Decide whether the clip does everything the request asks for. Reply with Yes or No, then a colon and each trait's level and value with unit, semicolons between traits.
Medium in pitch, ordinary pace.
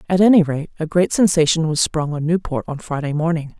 No: medium, 160 Hz; fast, 215 wpm